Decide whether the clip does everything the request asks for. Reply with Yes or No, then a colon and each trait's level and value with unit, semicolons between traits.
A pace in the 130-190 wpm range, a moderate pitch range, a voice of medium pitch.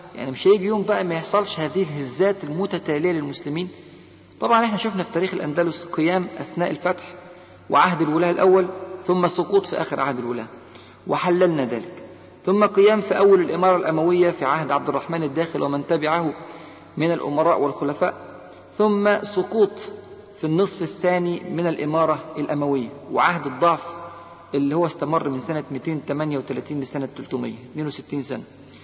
Yes: fast, 135 wpm; average, 3.7 semitones; medium, 170 Hz